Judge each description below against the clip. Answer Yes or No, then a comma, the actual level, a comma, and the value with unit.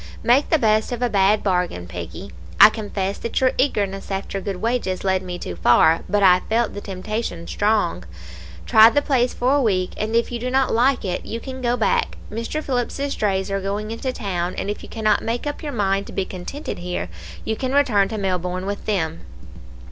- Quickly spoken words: Yes, fast, 210 wpm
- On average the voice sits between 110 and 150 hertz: No, high, 210 Hz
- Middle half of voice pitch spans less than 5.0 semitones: Yes, average, 4.2 semitones